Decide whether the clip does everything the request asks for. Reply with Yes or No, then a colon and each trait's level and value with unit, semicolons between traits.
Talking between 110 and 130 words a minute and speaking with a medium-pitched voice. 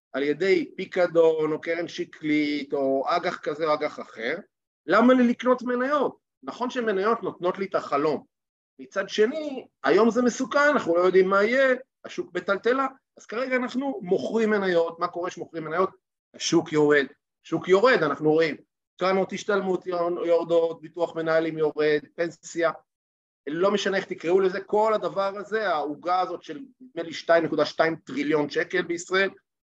No: fast, 150 wpm; medium, 180 Hz